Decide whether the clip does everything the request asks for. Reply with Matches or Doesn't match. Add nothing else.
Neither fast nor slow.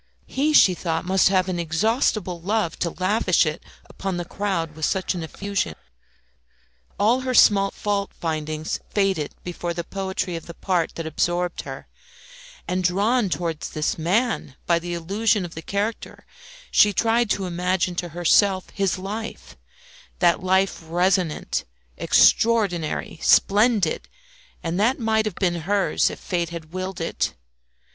Matches